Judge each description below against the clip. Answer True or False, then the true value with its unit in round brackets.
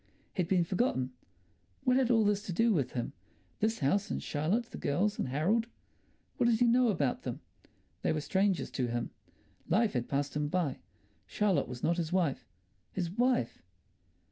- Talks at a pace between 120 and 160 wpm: False (170 wpm)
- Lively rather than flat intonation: True (7.5 semitones)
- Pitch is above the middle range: False (180 Hz)